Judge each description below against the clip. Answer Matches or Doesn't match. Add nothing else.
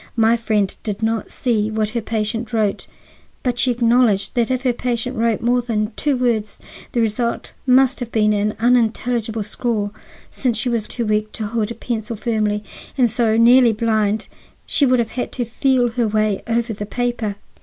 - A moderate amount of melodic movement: Doesn't match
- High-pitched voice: Matches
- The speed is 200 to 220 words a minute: Doesn't match